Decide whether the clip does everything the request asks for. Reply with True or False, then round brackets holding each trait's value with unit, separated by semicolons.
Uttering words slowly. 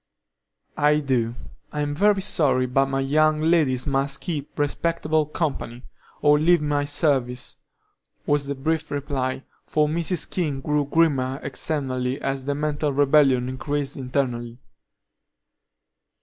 True (120 wpm)